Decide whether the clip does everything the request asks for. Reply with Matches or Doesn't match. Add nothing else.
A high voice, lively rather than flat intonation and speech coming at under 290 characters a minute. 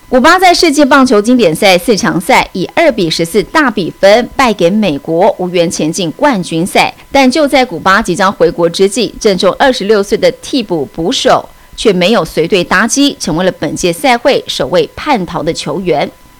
Matches